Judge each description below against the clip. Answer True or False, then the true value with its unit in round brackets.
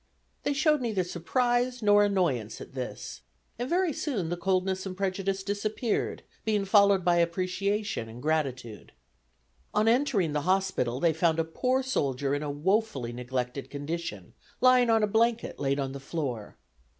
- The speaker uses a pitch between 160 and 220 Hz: True (185 Hz)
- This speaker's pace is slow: False (155 wpm)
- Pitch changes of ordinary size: False (7.2 semitones)